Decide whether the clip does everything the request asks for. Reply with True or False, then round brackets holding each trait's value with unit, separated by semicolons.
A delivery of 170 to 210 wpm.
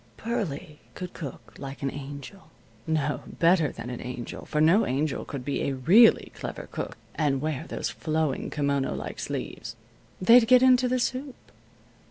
False (160 wpm)